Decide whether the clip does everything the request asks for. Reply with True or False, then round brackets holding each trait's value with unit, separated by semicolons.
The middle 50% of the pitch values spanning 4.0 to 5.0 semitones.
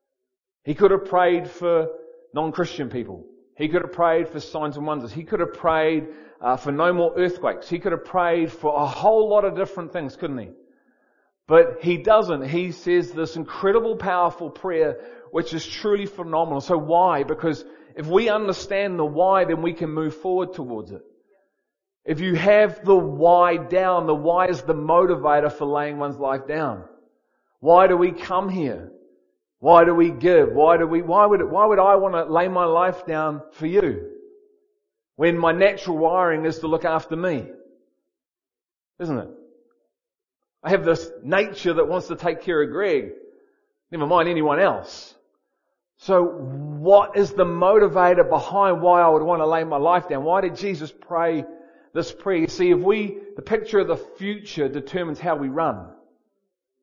False (3.5 semitones)